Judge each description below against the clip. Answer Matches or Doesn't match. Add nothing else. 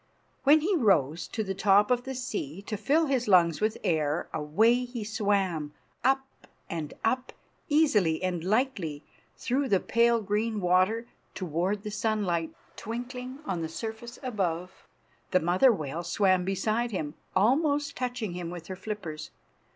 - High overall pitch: Matches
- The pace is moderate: Matches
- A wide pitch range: Matches